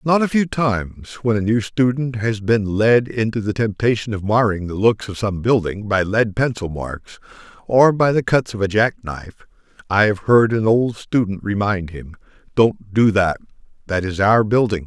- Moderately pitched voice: No, low, 110 Hz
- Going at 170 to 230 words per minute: Yes, average, 190 wpm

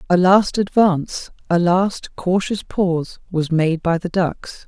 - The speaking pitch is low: No, medium, 180 Hz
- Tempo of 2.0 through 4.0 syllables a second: Yes, 3.8 syllables/s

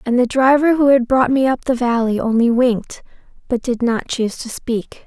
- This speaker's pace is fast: Yes, fast, 215 wpm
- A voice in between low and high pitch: No, high, 245 Hz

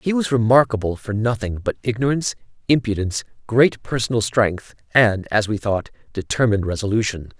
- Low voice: Yes, low, 110 Hz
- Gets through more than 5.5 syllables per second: Yes, 5.7 syllables/s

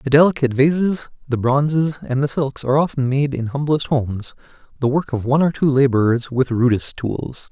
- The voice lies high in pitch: No, low, 135 Hz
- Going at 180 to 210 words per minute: Yes, average, 190 wpm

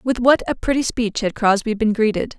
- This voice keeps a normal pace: No, fast, 225 wpm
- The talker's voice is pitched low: No, high, 230 Hz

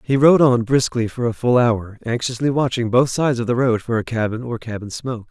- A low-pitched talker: Yes, low, 120 Hz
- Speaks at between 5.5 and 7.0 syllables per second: Yes, 5.6 syllables/s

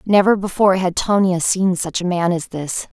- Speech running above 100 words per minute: Yes, average, 200 wpm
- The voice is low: No, medium, 185 Hz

